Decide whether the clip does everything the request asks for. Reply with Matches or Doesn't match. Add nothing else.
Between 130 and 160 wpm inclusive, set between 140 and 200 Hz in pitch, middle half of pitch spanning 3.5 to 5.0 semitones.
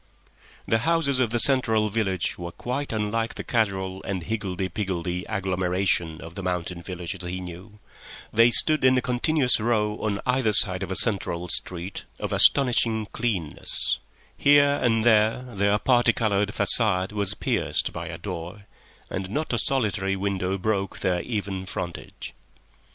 Doesn't match